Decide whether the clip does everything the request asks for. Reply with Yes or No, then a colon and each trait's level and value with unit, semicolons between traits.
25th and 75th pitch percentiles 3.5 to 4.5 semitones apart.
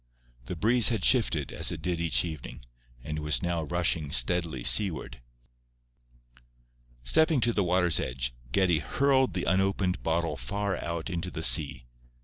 Yes: average, 4.1 semitones